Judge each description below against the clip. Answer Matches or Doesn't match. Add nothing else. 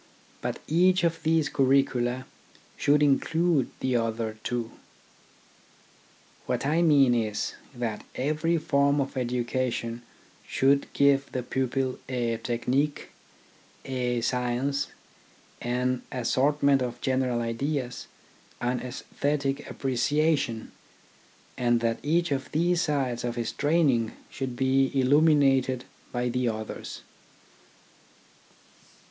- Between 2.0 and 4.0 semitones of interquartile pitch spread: Matches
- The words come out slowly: Matches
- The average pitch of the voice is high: Doesn't match